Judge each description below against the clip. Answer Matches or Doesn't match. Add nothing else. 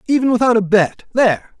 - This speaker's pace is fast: Doesn't match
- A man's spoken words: Matches